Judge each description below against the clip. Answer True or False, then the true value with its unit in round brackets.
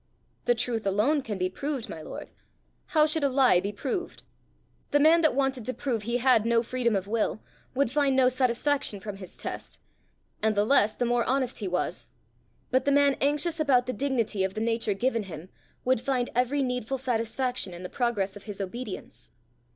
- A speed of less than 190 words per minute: False (195 wpm)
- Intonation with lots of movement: False (4.3 semitones)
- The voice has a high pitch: True (245 Hz)